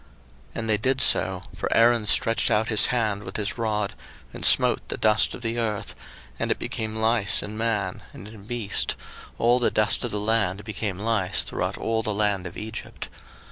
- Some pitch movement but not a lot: No, narrow, 1.8 semitones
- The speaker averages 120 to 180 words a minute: No, average, 195 wpm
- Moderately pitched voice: No, low, 110 Hz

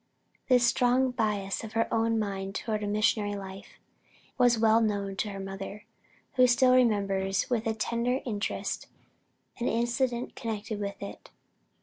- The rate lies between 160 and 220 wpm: No, average, 140 wpm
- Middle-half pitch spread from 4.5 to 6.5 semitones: No, average, 3.0 semitones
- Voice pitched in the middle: No, high, 220 Hz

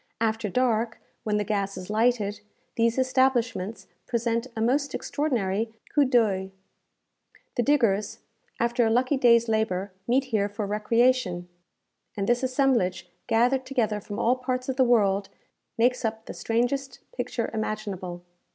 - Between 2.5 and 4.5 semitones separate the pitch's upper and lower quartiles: Yes, average, 3.4 semitones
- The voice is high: Yes, high, 230 Hz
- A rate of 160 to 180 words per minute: No, average, 140 wpm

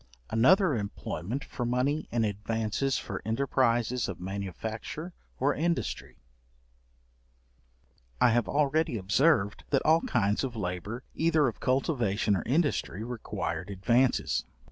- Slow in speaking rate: Yes, slow, 115 wpm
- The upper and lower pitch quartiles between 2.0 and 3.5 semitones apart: No, average, 5.1 semitones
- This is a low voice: Yes, low, 120 Hz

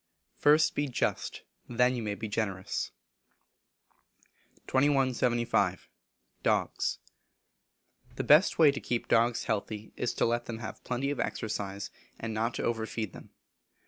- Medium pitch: No, low, 120 Hz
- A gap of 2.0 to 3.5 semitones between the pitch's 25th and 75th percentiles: Yes, average, 2.9 semitones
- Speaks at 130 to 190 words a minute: Yes, slow, 135 wpm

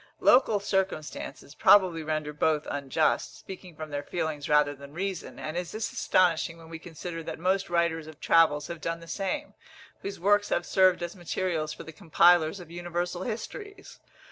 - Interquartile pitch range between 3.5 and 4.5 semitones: No, average, 3.1 semitones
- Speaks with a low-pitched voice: No, medium, 170 Hz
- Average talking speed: Yes, average, 170 wpm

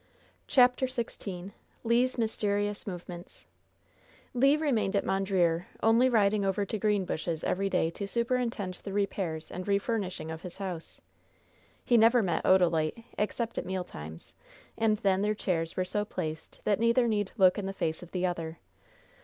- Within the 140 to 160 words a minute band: Yes, average, 155 wpm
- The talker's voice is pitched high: Yes, high, 200 Hz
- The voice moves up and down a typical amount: Yes, average, 3.8 semitones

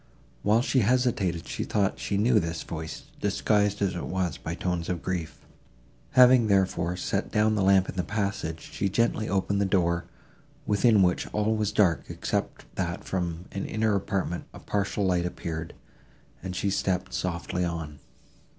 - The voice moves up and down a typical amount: Yes, average, 3.1 semitones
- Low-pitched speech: Yes, very low, 95 Hz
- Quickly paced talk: No, average, 165 wpm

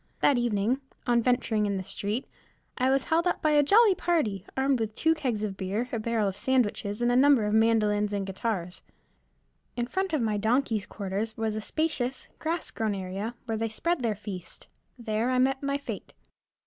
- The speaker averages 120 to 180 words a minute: No, average, 195 wpm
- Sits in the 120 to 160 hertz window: No, high, 230 Hz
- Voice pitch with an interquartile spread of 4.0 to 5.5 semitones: Yes, average, 4.4 semitones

